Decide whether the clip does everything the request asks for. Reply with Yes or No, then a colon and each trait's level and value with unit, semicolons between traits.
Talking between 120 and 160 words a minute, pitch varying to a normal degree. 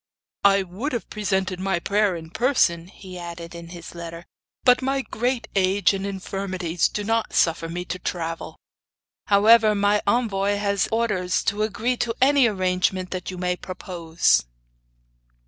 Yes: average, 150 wpm; average, 3.1 semitones